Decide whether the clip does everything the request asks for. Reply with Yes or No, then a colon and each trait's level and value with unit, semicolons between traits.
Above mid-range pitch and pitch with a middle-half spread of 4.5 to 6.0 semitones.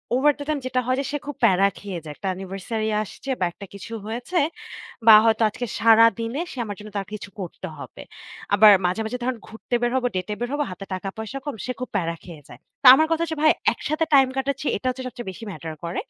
Yes: high, 225 Hz; average, 5.0 semitones